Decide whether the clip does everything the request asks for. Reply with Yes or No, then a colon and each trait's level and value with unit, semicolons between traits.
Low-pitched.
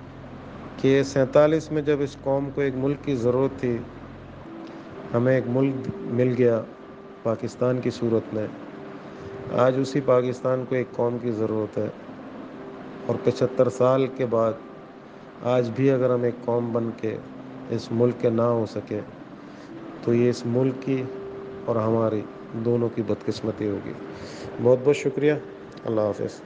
Yes: low, 120 Hz